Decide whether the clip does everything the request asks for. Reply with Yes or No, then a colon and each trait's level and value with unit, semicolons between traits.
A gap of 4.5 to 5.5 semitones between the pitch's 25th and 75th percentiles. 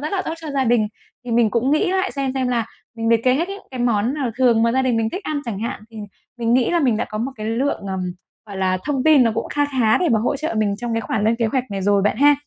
No: average, 3.9 semitones